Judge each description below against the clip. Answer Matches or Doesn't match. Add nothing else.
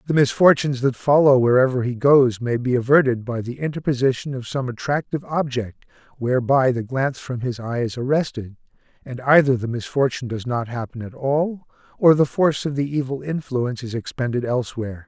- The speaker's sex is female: Doesn't match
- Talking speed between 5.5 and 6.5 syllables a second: Matches